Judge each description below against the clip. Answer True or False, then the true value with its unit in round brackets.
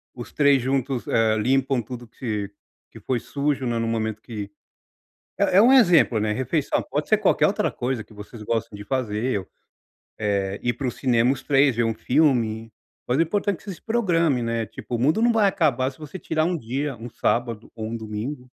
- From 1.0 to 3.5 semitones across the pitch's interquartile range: False (4.4 semitones)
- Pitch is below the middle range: True (125 Hz)